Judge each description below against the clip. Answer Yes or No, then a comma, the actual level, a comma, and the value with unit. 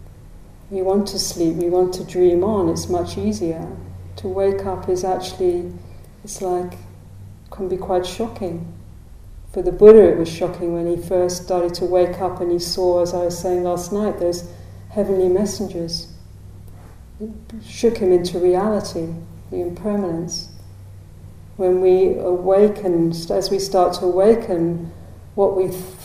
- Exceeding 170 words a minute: No, average, 150 wpm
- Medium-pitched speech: Yes, medium, 175 Hz